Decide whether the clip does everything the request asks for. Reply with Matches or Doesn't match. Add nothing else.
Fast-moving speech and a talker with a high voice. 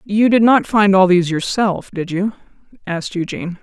Doesn't match